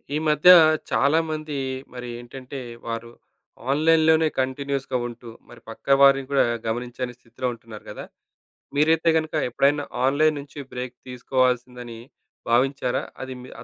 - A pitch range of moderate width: Yes, average, 3.0 semitones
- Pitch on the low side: Yes, low, 130 Hz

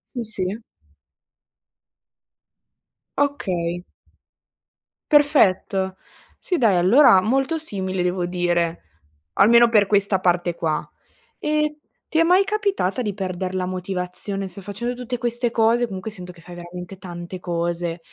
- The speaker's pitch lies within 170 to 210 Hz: Yes, high, 190 Hz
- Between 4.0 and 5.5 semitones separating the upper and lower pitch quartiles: Yes, average, 5.1 semitones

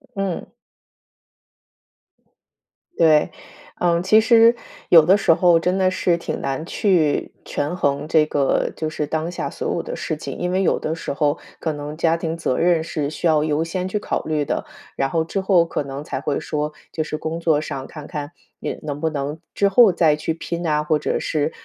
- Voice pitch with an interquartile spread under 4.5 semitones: Yes, average, 2.8 semitones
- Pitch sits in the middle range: Yes, medium, 160 Hz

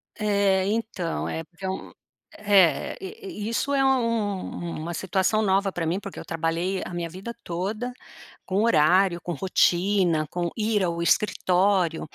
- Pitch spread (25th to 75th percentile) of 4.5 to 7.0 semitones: No, average, 3.5 semitones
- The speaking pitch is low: No, high, 190 Hz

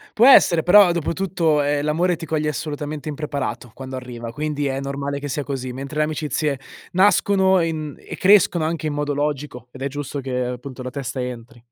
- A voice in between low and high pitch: Yes, medium, 145 Hz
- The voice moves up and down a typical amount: Yes, average, 3.1 semitones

